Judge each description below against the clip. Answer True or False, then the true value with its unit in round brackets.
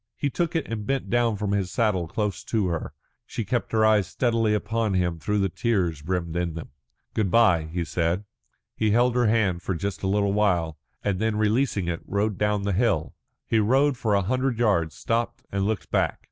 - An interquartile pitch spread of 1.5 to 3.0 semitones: False (3.9 semitones)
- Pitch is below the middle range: True (105 Hz)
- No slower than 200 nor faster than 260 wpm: True (205 wpm)